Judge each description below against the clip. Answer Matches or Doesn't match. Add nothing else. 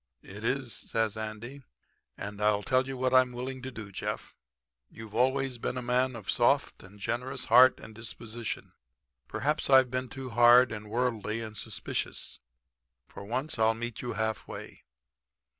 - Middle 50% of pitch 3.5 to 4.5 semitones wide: Doesn't match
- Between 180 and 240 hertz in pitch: Doesn't match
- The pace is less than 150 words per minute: Doesn't match